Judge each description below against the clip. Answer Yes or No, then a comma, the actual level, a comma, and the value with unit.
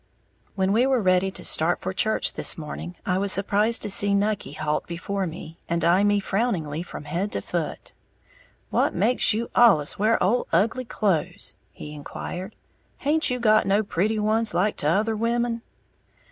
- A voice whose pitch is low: No, high, 200 Hz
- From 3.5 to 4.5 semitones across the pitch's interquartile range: Yes, average, 4.2 semitones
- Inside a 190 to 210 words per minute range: No, average, 175 wpm